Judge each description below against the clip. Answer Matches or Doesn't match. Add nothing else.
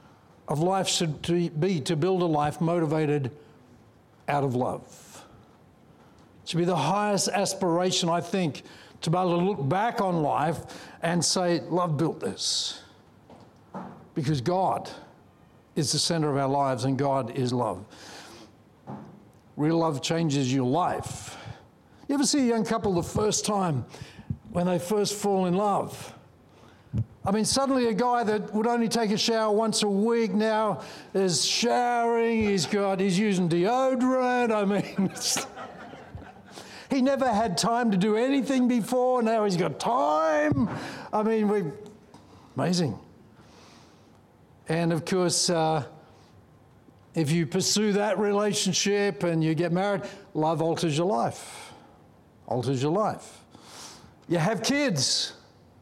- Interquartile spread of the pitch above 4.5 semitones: Matches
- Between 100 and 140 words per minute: Matches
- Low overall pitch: Doesn't match